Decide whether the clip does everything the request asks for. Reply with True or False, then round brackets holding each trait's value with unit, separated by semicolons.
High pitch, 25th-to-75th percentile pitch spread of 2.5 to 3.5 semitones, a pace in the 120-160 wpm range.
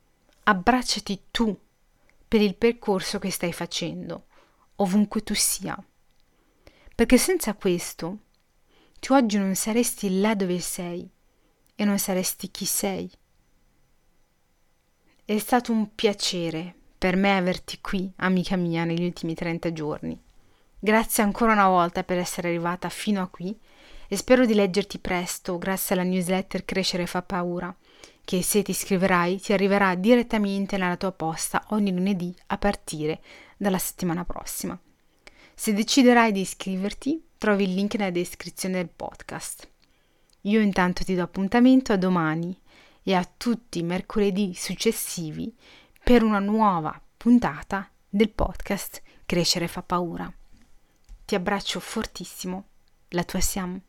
True (195 Hz; 2.9 semitones; 130 wpm)